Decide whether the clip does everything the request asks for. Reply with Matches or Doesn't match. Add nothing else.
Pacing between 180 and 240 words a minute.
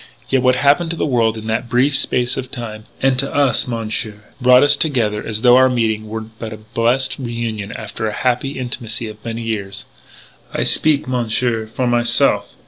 Matches